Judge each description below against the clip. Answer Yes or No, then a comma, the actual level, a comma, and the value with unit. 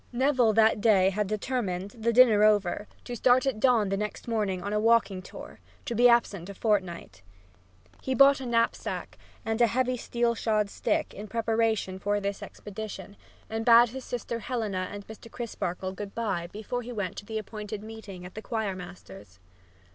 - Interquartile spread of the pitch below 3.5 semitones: Yes, average, 2.9 semitones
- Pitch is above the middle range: Yes, high, 215 Hz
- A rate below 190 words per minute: Yes, average, 180 wpm